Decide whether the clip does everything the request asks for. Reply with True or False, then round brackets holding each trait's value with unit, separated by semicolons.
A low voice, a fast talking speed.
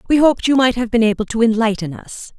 False (230 Hz; 250 wpm)